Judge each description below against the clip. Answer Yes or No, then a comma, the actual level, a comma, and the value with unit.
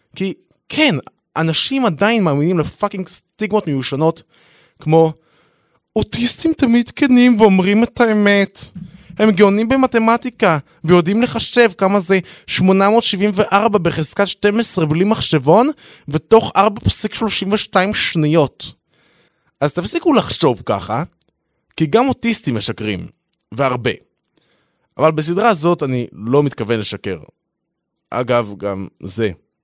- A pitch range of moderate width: No, wide, 5.8 semitones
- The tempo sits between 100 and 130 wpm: Yes, average, 105 wpm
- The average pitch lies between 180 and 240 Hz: Yes, high, 190 Hz